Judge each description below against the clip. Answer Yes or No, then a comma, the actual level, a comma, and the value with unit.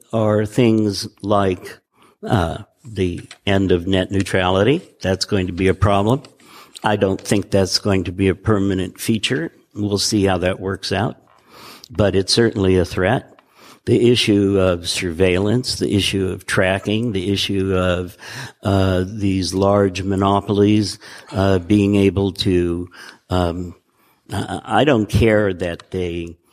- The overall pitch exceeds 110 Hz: No, low, 100 Hz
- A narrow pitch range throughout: Yes, narrow, 2.0 semitones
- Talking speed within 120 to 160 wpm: Yes, average, 140 wpm